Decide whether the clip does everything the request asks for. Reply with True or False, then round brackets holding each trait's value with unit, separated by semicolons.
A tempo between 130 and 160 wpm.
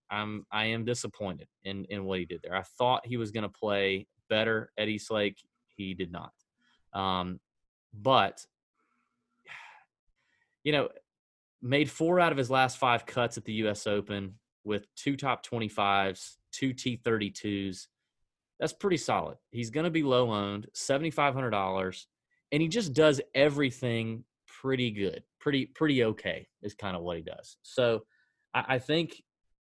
True (155 wpm)